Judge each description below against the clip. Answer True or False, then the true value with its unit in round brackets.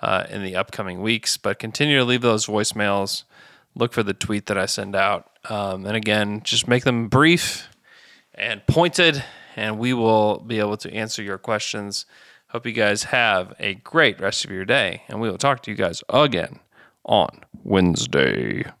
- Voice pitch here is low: True (110 Hz)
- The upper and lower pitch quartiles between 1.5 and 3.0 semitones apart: True (2.4 semitones)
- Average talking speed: True (180 wpm)